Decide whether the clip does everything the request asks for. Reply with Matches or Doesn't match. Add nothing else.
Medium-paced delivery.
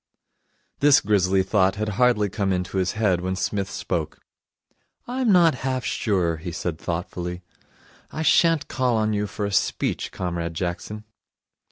Matches